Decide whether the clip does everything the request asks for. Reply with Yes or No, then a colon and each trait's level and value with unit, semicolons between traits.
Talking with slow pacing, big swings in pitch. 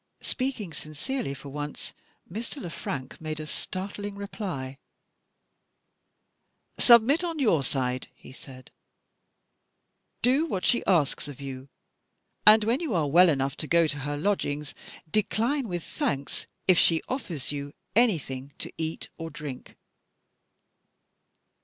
Yes: slow, 130 wpm; wide, 7.2 semitones